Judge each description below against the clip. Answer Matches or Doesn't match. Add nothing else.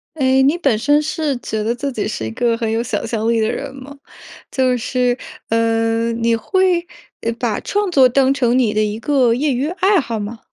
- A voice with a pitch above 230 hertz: Matches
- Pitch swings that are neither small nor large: Matches